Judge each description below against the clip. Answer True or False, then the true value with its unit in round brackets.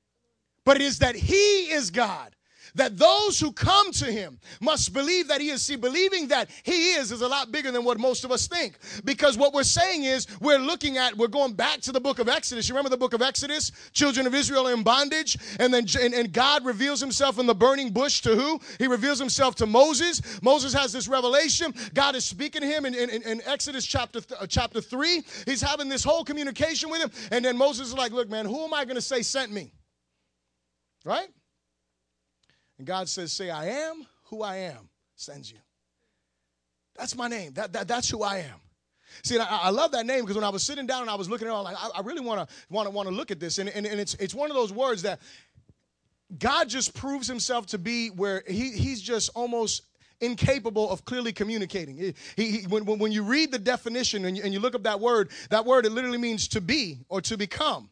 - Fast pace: True (230 wpm)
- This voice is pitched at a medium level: False (245 Hz)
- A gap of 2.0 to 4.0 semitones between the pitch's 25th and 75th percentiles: False (4.8 semitones)